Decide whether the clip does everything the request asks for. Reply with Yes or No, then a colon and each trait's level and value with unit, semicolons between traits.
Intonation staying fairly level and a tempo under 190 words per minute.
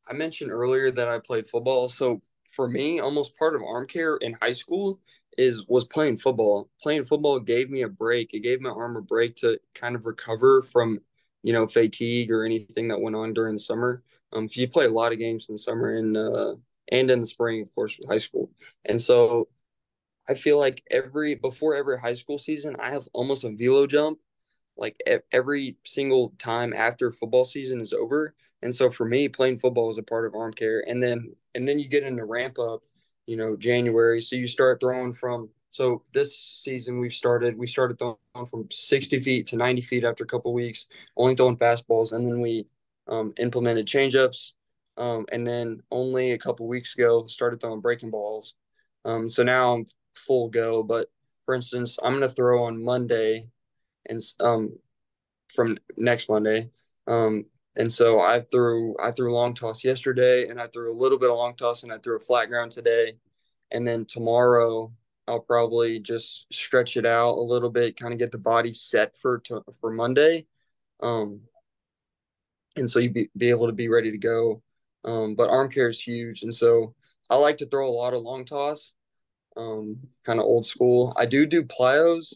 No: narrow, 2.3 semitones; average, 200 wpm